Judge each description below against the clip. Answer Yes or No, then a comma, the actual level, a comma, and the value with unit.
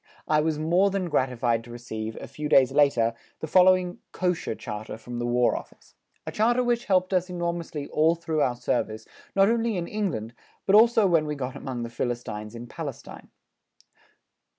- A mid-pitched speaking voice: Yes, medium, 150 Hz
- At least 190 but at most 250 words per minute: No, average, 175 wpm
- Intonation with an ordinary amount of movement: No, wide, 7.3 semitones